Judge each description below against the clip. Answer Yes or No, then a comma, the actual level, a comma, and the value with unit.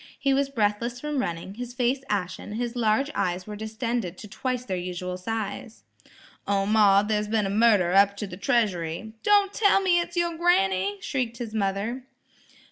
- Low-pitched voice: No, high, 220 Hz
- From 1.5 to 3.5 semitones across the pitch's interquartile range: No, average, 4.2 semitones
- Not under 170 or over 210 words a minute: Yes, average, 175 wpm